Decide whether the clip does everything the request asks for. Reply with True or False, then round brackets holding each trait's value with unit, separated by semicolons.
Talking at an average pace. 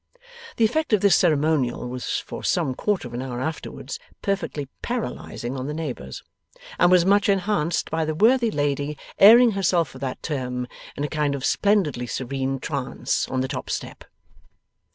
True (170 wpm)